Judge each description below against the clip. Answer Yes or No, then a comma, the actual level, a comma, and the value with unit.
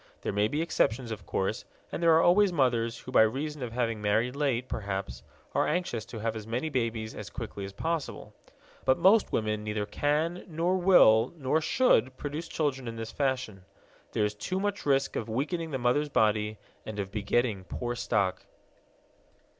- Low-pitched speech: Yes, low, 120 Hz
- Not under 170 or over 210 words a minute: Yes, average, 180 wpm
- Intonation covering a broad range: Yes, wide, 5.7 semitones